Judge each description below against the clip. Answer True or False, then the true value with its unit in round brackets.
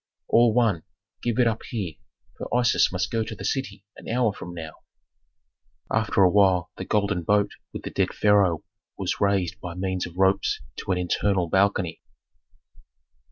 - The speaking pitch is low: True (100 Hz)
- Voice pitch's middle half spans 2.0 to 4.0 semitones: True (3.2 semitones)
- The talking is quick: False (165 wpm)